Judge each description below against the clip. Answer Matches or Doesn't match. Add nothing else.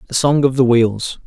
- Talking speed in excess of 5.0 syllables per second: Doesn't match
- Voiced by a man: Matches